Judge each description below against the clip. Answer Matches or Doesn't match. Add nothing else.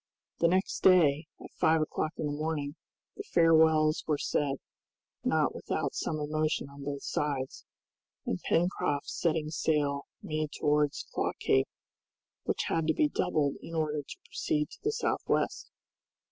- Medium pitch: Matches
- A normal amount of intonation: Doesn't match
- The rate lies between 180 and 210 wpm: Doesn't match